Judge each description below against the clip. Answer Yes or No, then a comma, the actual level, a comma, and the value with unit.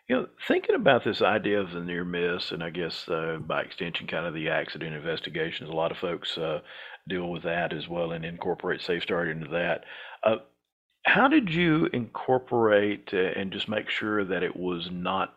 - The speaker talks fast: No, average, 190 wpm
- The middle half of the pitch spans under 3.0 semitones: No, average, 4.4 semitones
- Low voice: Yes, very low, 95 Hz